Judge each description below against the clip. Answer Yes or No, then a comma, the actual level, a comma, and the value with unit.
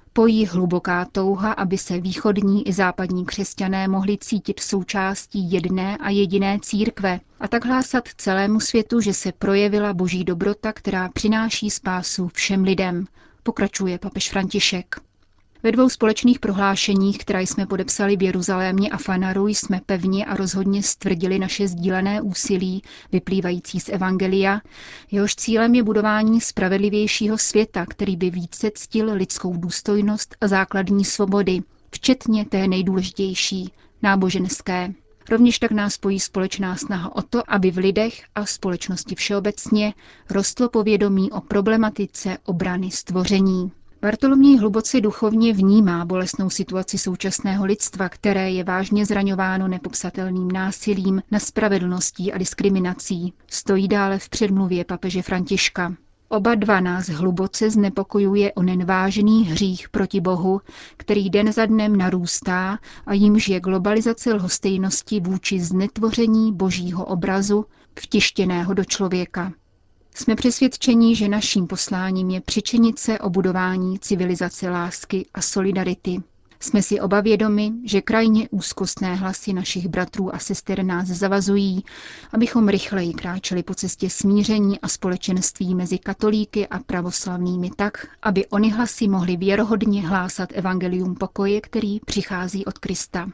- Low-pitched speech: No, high, 195 Hz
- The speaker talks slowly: No, average, 125 wpm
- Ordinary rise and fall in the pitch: No, narrow, 2.1 semitones